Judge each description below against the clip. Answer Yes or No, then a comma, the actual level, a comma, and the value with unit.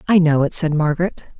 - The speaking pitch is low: No, medium, 160 Hz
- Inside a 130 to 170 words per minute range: No, fast, 215 wpm